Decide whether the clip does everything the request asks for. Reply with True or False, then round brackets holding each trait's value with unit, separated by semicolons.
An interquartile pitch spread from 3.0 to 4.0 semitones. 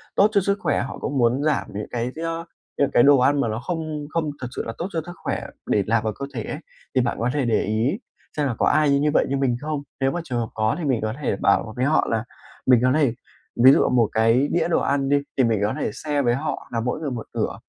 False (4.4 semitones)